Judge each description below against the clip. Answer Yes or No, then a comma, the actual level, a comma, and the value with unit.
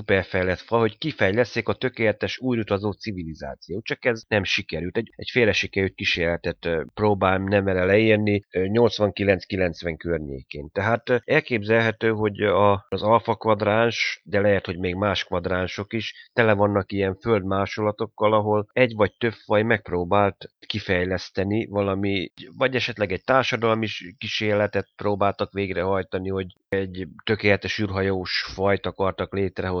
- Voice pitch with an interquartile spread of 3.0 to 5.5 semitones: No, narrow, 2.5 semitones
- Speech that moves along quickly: No, average, 120 wpm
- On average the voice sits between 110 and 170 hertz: No, low, 100 Hz